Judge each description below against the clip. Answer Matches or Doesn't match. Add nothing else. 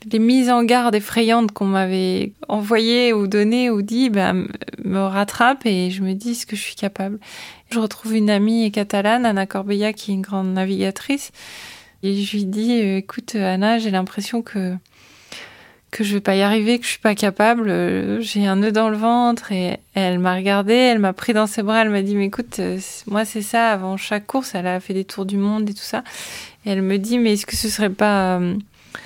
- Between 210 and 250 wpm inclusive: Matches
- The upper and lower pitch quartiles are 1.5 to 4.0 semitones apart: Matches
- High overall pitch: Matches